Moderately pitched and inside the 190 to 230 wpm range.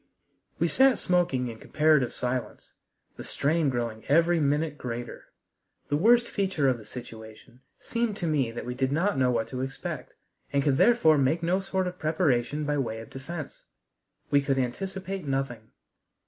No: medium, 145 Hz; average, 165 wpm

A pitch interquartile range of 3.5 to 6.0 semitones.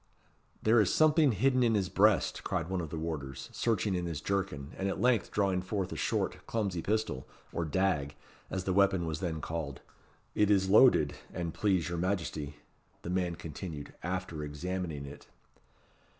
Yes: average, 3.9 semitones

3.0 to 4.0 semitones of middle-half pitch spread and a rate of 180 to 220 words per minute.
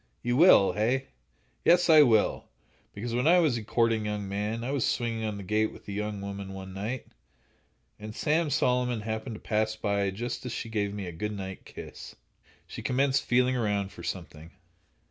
Yes: average, 3.6 semitones; average, 190 wpm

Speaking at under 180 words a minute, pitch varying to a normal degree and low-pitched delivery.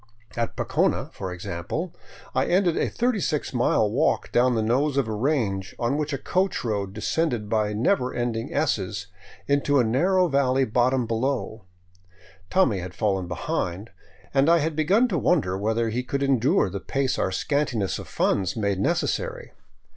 No: average, 160 wpm; wide, 6.2 semitones; low, 125 Hz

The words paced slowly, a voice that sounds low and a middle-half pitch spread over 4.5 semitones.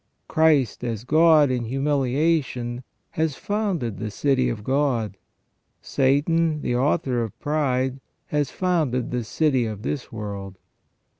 No: slow, 125 wpm; low, 130 Hz; average, 4.1 semitones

